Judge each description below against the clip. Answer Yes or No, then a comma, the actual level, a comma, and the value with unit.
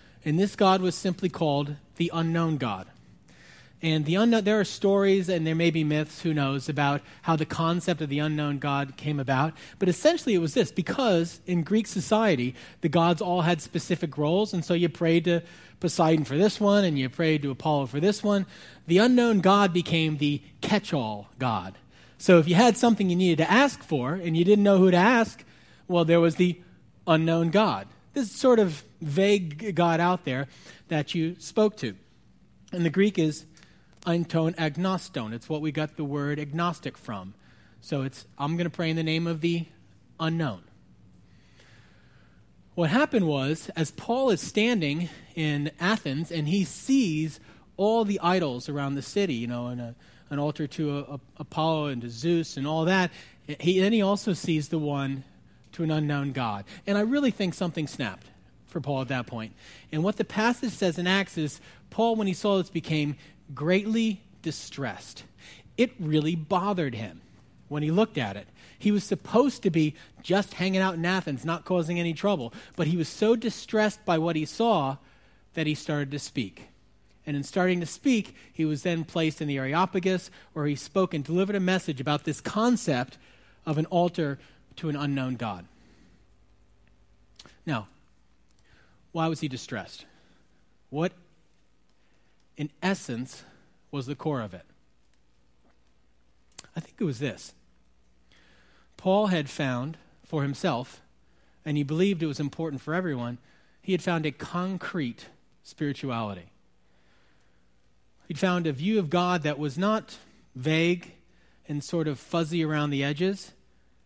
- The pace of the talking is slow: No, average, 170 wpm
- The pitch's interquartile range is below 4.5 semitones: No, average, 4.8 semitones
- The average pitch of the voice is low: No, medium, 160 Hz